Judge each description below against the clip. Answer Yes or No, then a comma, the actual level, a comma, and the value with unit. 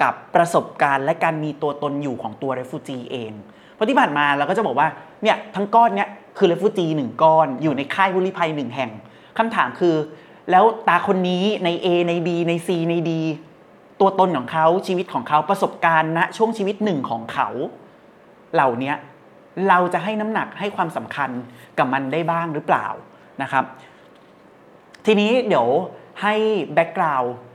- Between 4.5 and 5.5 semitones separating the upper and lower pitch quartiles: Yes, average, 4.8 semitones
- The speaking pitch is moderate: Yes, medium, 170 Hz